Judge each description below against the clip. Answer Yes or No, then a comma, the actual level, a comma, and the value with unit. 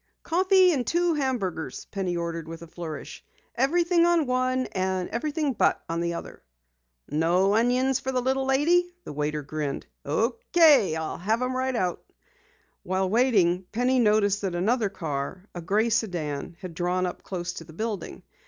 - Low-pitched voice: No, high, 205 Hz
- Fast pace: No, average, 160 wpm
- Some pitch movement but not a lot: No, wide, 7.1 semitones